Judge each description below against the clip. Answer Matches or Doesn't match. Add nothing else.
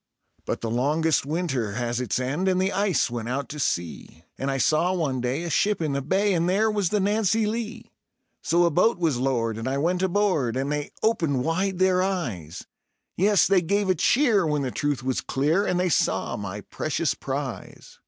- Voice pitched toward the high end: Doesn't match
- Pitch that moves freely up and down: Matches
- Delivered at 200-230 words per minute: Matches